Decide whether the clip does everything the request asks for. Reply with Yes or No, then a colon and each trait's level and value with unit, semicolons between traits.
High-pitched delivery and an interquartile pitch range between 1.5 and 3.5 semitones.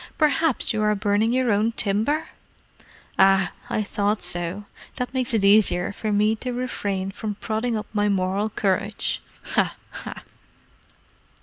Yes: high, 210 Hz; narrow, 2.6 semitones